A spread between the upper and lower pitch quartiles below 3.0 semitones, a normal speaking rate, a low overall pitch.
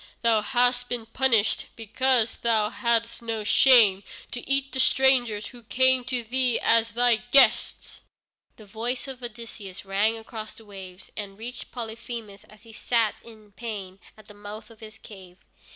No: narrow, 2.5 semitones; average, 160 wpm; high, 230 Hz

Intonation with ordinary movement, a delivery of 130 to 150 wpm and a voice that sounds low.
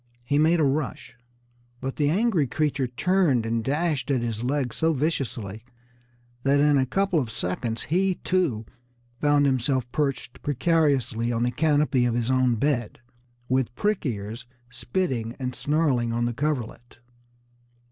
Yes: average, 4.1 semitones; average, 145 wpm; low, 130 Hz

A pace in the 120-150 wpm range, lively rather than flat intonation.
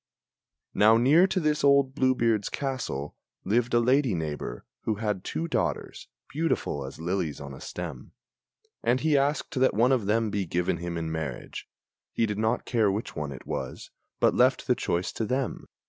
No: average, 180 wpm; wide, 7.3 semitones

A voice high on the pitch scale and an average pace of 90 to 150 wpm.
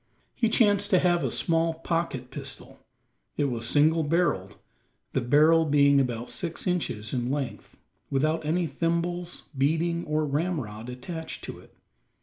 No: medium, 155 Hz; average, 140 wpm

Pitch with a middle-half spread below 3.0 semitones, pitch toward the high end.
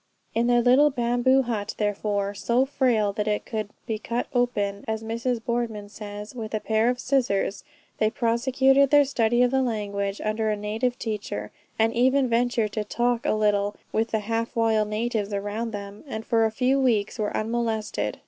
Yes: narrow, 2.6 semitones; high, 225 Hz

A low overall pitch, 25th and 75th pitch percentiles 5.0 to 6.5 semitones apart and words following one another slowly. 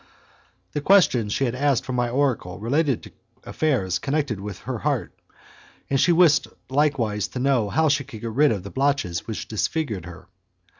No: low, 130 Hz; wide, 5.5 semitones; average, 180 wpm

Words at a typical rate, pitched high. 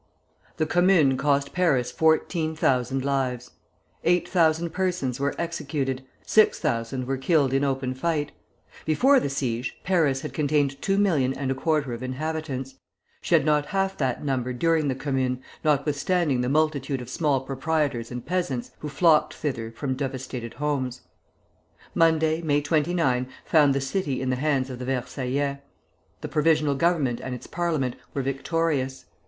No: average, 155 wpm; medium, 140 Hz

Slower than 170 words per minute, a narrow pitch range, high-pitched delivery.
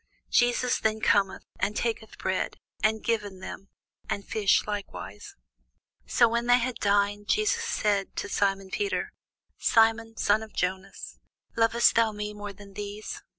Yes: average, 145 wpm; narrow, 2.3 semitones; high, 210 Hz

